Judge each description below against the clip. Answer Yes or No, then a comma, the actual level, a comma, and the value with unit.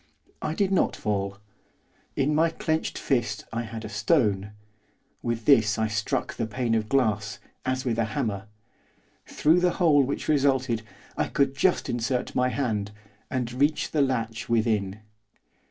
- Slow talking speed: No, average, 155 wpm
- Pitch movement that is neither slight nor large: Yes, average, 4.3 semitones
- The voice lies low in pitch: Yes, low, 120 Hz